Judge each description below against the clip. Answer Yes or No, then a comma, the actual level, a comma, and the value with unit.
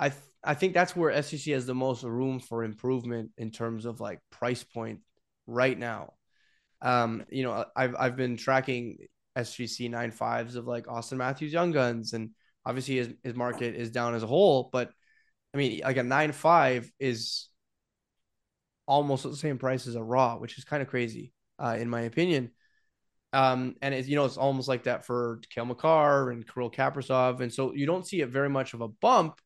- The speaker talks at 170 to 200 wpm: Yes, average, 195 wpm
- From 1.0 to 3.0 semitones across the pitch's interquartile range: Yes, narrow, 2.6 semitones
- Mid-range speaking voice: No, low, 125 Hz